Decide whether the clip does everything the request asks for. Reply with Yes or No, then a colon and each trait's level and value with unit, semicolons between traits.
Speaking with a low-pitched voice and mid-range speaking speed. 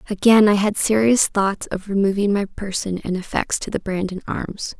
No: high, 200 Hz; average, 190 wpm